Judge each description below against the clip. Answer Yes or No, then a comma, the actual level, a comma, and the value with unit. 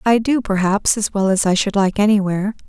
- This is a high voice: Yes, high, 205 Hz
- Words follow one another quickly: Yes, fast, 225 wpm